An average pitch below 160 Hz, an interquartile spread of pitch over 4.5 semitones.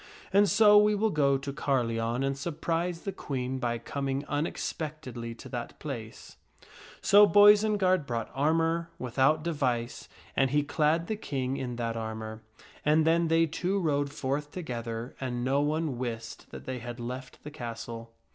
Yes: medium, 140 Hz; average, 5.2 semitones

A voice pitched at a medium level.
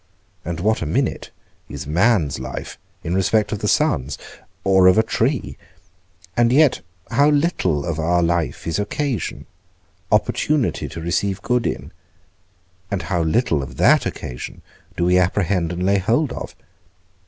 No: very low, 95 Hz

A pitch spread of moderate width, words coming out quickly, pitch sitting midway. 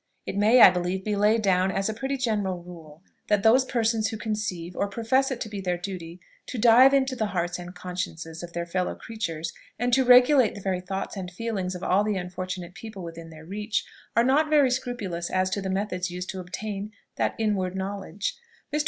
No: average, 3.8 semitones; fast, 210 wpm; high, 195 Hz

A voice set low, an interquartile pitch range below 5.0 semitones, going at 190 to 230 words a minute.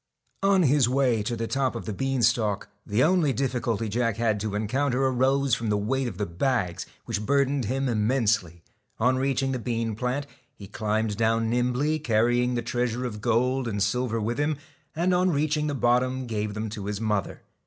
Yes: low, 120 Hz; average, 3.6 semitones; average, 195 wpm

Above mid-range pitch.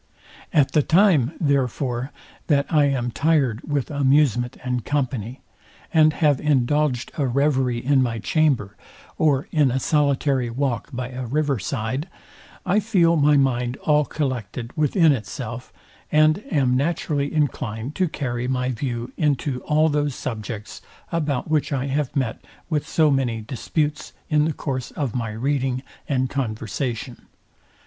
No: low, 135 Hz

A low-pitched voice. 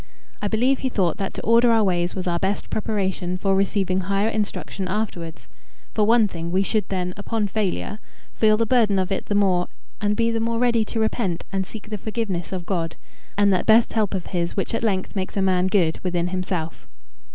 No: high, 195 Hz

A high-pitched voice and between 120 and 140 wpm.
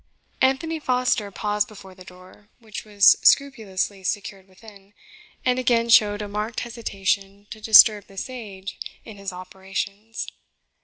Yes: high, 205 Hz; slow, 135 wpm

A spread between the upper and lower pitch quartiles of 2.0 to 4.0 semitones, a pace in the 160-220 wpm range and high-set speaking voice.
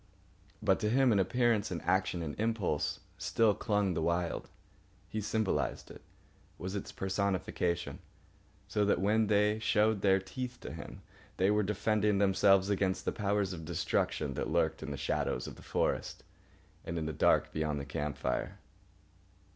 No: average, 3.6 semitones; average, 165 wpm; very low, 95 Hz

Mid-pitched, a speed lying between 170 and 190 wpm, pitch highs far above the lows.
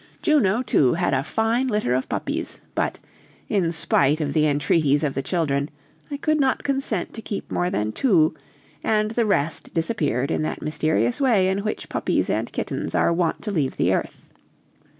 Yes: medium, 175 Hz; average, 180 wpm; wide, 7.2 semitones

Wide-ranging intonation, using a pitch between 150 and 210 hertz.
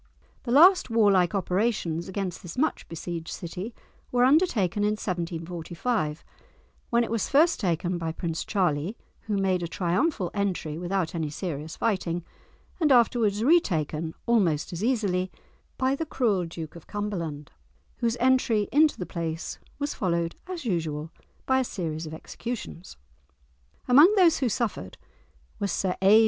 Yes: wide, 5.9 semitones; high, 190 Hz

